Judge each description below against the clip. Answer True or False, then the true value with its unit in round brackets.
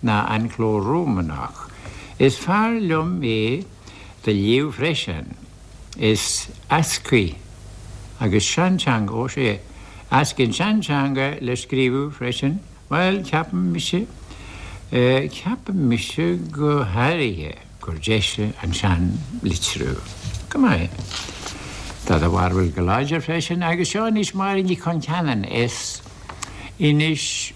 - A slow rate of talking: True (110 wpm)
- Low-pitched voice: True (125 Hz)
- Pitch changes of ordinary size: False (8.1 semitones)